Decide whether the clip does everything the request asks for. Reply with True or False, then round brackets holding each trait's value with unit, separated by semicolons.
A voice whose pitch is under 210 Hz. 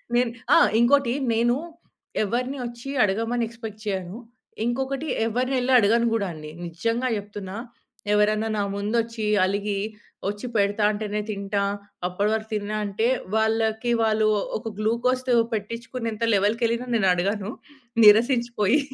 False (220 Hz)